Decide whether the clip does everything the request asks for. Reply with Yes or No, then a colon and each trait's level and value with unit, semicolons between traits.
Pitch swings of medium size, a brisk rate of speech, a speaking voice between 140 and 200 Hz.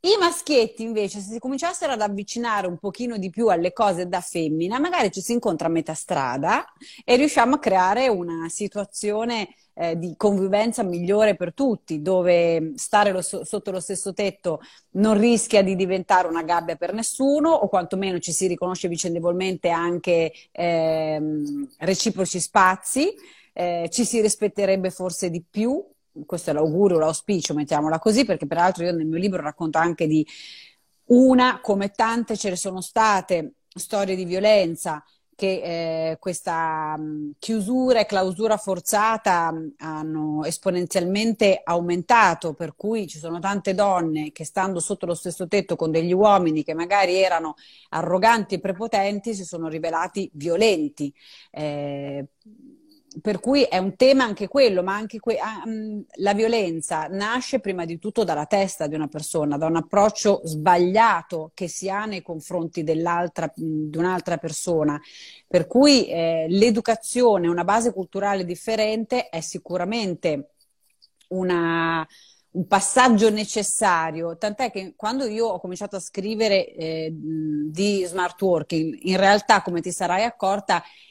No: average, 4.3 semitones; average, 145 wpm; medium, 185 Hz